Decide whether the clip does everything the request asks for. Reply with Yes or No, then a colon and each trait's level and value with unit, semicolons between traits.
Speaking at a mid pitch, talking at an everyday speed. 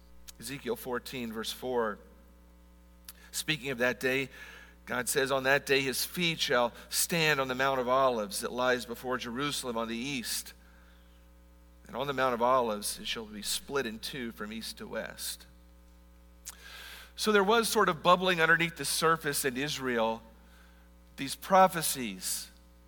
No: low, 125 Hz; average, 150 wpm